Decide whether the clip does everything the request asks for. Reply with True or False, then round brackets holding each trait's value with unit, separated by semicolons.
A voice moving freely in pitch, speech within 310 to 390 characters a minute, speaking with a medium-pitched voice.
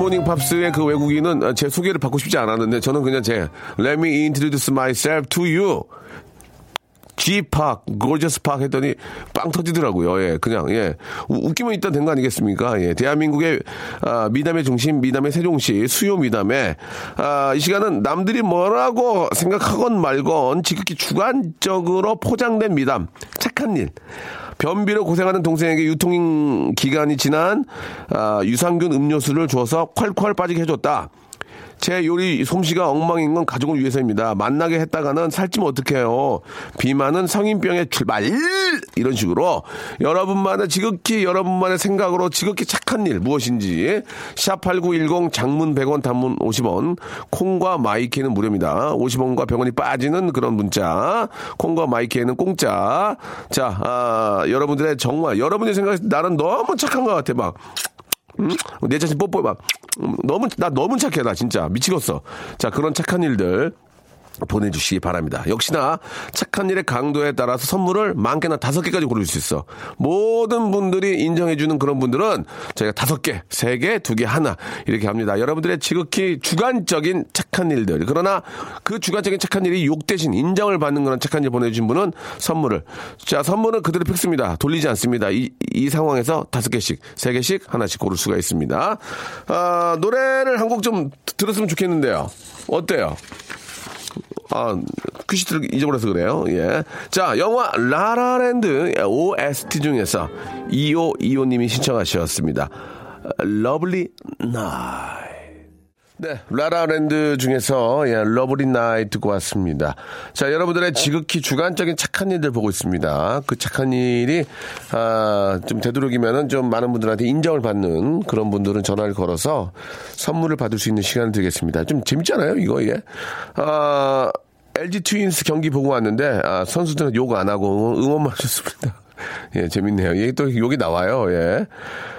True (6.5 semitones; 325 characters per minute; 150 Hz)